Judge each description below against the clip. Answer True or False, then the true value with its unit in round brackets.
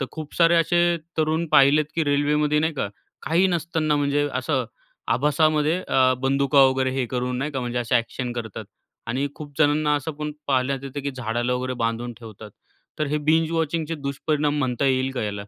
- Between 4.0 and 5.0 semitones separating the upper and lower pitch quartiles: False (3.2 semitones)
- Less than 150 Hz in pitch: True (140 Hz)